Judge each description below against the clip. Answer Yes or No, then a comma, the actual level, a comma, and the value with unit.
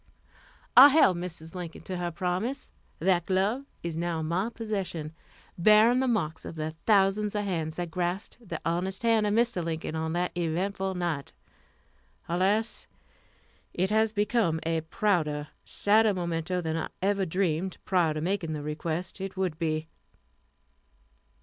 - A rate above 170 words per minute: No, average, 150 wpm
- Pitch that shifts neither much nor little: Yes, average, 3.9 semitones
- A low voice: No, medium, 180 Hz